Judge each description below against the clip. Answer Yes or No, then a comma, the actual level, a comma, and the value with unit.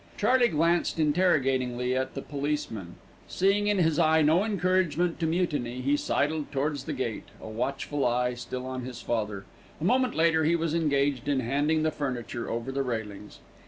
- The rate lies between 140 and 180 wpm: Yes, average, 170 wpm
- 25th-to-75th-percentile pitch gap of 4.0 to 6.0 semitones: Yes, average, 4.6 semitones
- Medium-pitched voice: Yes, medium, 145 Hz